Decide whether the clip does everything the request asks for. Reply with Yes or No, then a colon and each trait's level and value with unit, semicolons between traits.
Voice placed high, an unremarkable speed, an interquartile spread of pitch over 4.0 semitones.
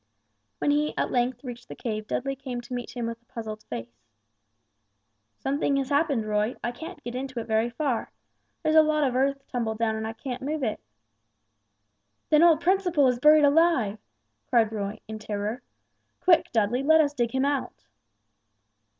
Yes: very high, 250 Hz; average, 175 wpm; average, 4.5 semitones